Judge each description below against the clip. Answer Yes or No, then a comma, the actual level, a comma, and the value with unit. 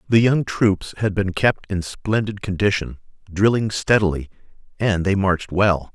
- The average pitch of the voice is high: No, low, 100 Hz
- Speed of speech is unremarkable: Yes, average, 150 wpm